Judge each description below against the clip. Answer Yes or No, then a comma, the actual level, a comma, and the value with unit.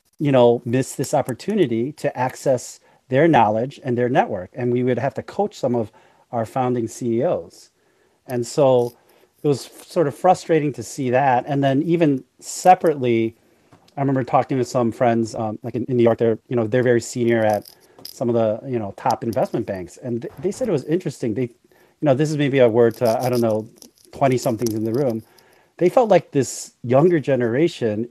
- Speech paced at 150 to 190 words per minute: No, average, 200 wpm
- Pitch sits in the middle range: No, low, 125 Hz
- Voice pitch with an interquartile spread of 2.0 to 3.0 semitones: No, average, 3.6 semitones